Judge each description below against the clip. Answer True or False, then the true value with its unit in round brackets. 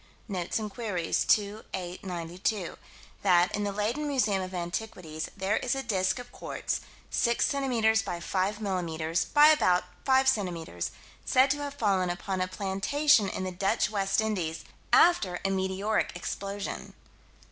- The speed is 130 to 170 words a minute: True (150 wpm)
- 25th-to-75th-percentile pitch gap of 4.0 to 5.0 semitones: False (3.5 semitones)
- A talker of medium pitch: False (195 Hz)